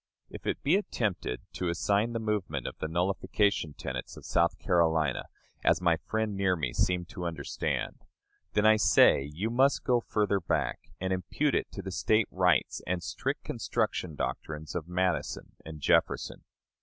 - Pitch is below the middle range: Yes, very low, 90 Hz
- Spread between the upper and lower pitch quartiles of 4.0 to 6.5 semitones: Yes, average, 4.5 semitones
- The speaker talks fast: No, average, 165 wpm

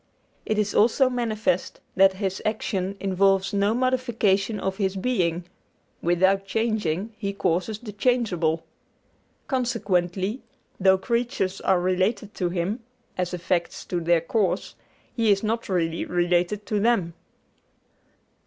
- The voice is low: No, high, 195 Hz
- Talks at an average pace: No, slow, 125 wpm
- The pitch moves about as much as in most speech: Yes, average, 3.5 semitones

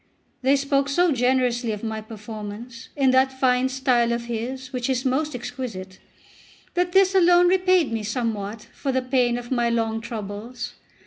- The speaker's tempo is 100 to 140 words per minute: No, average, 165 wpm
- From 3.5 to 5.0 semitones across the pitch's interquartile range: No, average, 2.8 semitones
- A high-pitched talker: Yes, very high, 250 Hz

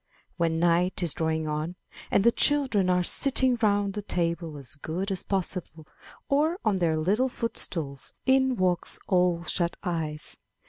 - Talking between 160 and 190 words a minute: No, average, 150 wpm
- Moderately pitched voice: Yes, medium, 180 Hz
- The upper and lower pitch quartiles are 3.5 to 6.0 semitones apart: Yes, average, 4.3 semitones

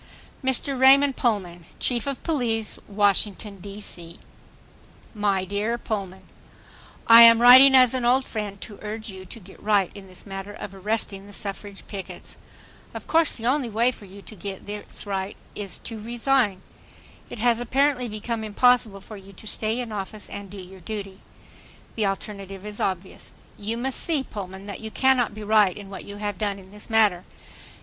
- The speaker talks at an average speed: Yes, average, 175 wpm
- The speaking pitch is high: Yes, high, 210 Hz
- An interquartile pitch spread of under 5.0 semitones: Yes, average, 3.2 semitones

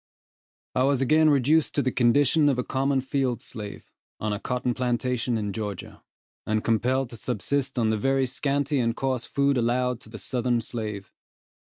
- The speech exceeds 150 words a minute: Yes, average, 175 wpm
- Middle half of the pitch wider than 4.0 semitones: No, average, 2.8 semitones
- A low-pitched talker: Yes, low, 125 Hz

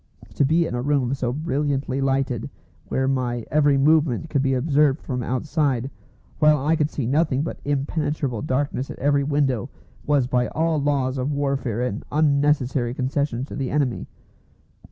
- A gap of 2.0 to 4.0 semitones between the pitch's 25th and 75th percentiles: Yes, narrow, 2.4 semitones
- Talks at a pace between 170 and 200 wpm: No, average, 160 wpm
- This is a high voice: No, medium, 140 Hz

